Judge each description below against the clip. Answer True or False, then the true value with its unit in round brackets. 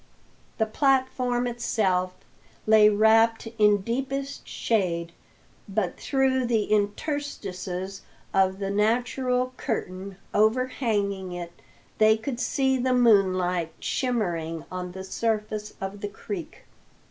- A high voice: True (215 Hz)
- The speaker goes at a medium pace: False (105 wpm)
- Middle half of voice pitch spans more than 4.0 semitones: True (4.5 semitones)